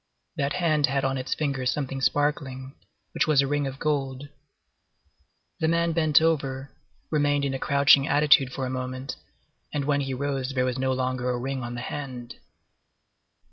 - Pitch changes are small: Yes, narrow, 2.0 semitones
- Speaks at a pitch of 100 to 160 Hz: Yes, low, 135 Hz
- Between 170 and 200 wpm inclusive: Yes, average, 175 wpm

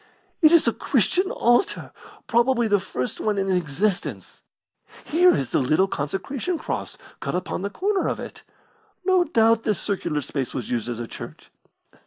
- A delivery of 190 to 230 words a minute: No, average, 165 wpm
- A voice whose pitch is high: Yes, high, 210 Hz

